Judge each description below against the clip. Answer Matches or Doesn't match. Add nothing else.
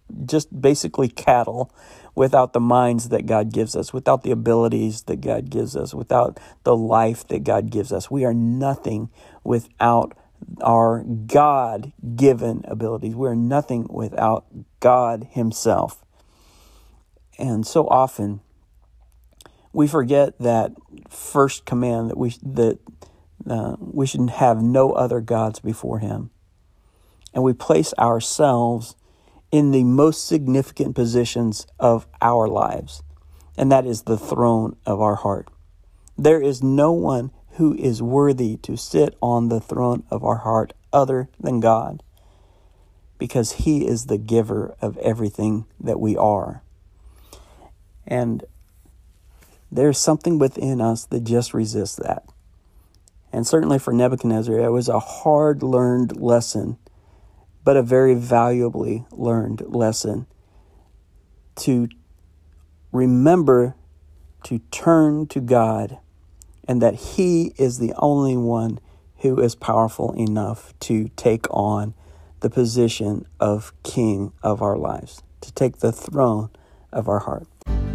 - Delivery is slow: Matches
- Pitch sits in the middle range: Doesn't match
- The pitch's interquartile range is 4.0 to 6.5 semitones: Matches